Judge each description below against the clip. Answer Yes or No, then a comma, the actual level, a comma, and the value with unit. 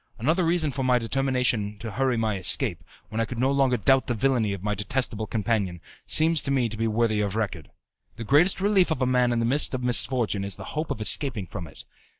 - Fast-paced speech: Yes, fast, 230 wpm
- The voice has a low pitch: Yes, low, 120 Hz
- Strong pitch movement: No, average, 4.1 semitones